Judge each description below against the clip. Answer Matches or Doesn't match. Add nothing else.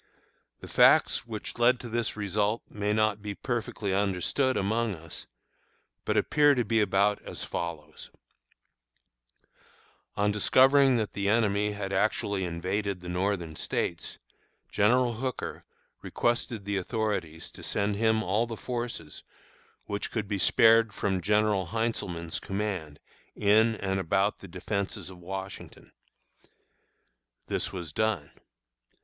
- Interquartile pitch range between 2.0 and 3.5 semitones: Matches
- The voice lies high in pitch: Doesn't match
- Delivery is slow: Matches